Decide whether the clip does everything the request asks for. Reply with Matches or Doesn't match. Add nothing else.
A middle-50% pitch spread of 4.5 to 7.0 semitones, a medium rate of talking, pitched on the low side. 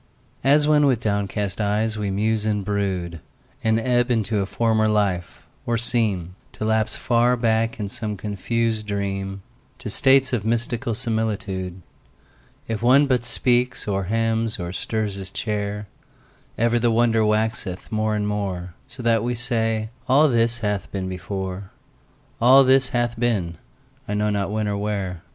Doesn't match